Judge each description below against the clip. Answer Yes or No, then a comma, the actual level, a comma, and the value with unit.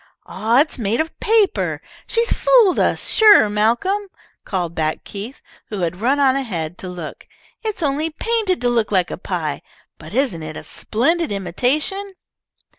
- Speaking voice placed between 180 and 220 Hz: No, high, 245 Hz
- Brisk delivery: No, average, 165 wpm